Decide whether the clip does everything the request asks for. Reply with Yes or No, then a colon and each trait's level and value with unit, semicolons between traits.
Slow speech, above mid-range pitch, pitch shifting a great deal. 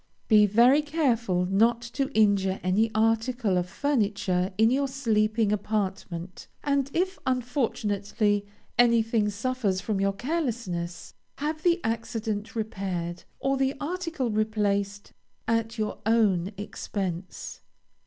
No: slow, 115 wpm; high, 220 Hz; average, 4.1 semitones